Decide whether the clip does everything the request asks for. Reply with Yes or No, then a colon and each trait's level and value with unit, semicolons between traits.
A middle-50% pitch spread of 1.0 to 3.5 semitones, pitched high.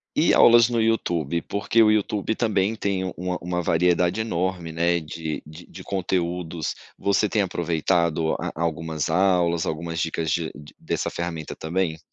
No: average, 2.7 semitones; very low, 85 Hz